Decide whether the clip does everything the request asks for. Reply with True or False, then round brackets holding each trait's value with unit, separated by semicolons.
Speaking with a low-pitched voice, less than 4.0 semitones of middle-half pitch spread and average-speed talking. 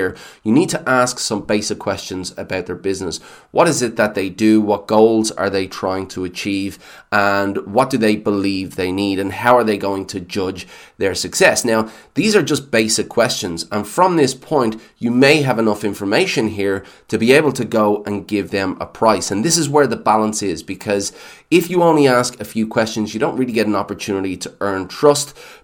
False (105 Hz; 2.6 semitones; 210 wpm)